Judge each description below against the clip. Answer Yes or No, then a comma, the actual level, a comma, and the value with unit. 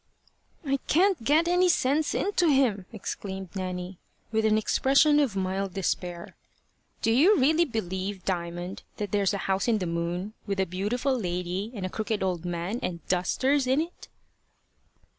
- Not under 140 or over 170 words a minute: Yes, average, 160 wpm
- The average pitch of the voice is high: Yes, high, 200 Hz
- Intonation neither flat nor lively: No, wide, 6.6 semitones